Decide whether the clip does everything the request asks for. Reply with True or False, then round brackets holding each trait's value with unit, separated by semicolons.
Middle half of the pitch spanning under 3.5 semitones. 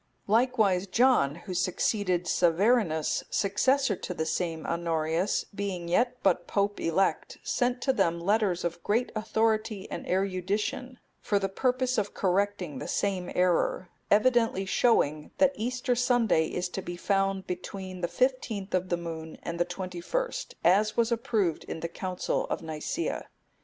False (4.6 semitones)